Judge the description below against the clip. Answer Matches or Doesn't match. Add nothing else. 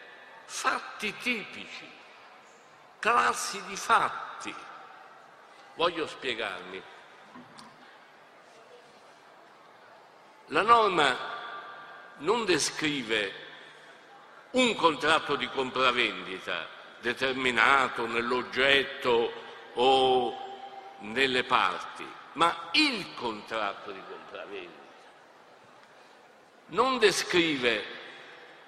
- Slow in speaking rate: Matches